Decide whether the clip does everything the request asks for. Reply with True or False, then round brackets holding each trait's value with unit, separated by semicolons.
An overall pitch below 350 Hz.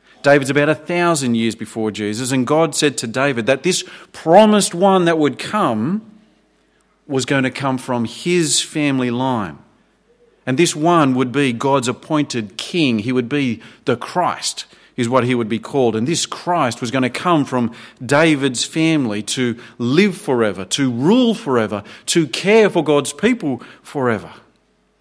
True (140 Hz)